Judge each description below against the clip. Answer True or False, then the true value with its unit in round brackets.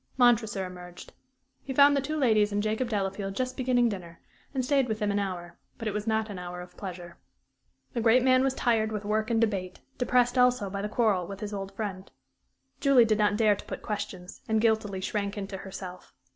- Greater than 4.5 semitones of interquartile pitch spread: False (3.6 semitones)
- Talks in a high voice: True (210 Hz)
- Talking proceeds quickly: True (210 wpm)